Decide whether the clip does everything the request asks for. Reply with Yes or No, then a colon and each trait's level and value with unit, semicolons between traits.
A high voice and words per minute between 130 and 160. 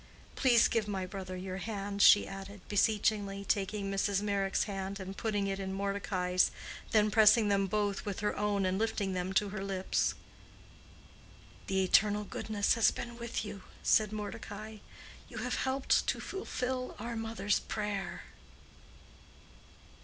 Yes: high, 205 Hz; average, 145 wpm